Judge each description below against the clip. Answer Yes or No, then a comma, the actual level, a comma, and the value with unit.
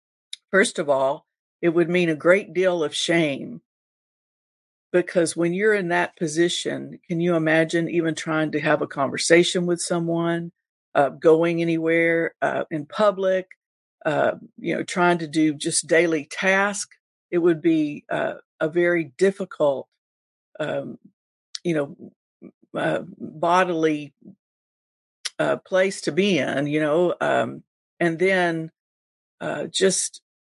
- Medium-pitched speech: Yes, medium, 170 Hz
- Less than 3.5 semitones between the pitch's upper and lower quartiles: Yes, narrow, 2.6 semitones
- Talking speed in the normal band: No, slow, 130 wpm